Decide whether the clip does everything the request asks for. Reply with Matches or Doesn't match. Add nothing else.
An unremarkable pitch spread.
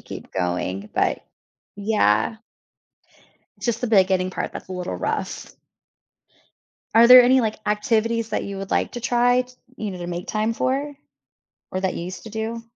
Matches